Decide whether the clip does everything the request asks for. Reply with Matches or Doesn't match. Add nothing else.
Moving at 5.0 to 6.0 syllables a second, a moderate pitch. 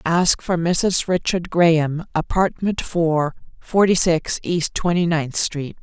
Doesn't match